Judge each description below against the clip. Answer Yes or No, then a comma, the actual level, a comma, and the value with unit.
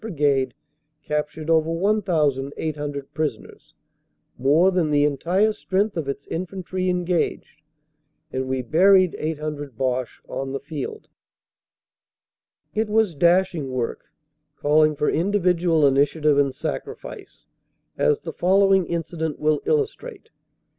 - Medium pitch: Yes, medium, 160 Hz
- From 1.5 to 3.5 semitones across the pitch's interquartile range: No, average, 4.5 semitones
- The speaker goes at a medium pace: No, slow, 110 wpm